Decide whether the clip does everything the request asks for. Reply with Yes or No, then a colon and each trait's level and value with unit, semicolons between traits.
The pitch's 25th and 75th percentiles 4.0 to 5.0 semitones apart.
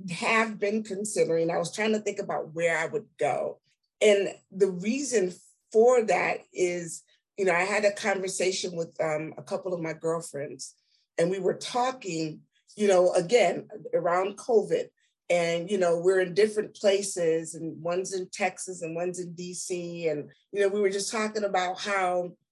No: average, 3.1 semitones